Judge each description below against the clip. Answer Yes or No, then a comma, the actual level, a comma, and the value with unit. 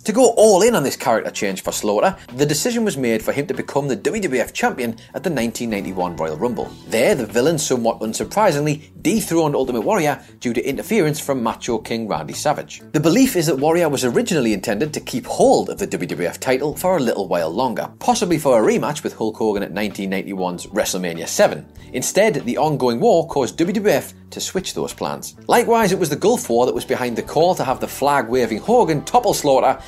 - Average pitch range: No, wide, 6.1 semitones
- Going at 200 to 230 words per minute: Yes, fast, 205 wpm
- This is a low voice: Yes, low, 130 Hz